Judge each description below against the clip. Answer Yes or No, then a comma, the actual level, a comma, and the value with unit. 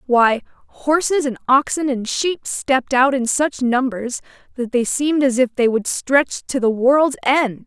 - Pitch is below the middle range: No, very high, 260 Hz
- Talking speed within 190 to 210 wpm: No, average, 180 wpm